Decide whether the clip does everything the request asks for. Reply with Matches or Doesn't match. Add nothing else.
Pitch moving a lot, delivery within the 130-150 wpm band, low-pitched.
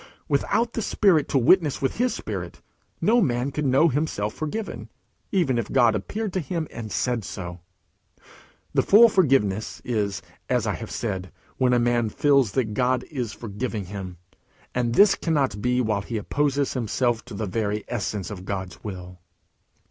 Doesn't match